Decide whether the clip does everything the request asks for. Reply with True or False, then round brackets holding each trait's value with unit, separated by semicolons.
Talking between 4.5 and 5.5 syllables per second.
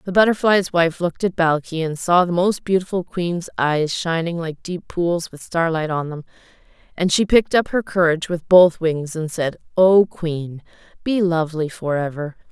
True (4.8 syllables/s)